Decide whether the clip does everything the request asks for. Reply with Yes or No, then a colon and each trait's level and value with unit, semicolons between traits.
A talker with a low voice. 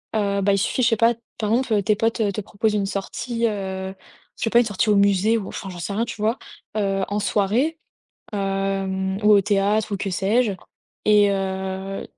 No: high, 200 Hz